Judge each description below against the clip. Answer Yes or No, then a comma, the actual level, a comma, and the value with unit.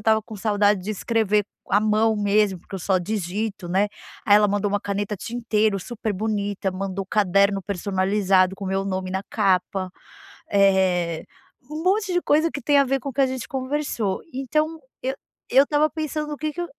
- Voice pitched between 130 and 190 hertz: No, high, 210 Hz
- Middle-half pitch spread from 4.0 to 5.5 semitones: Yes, average, 4.9 semitones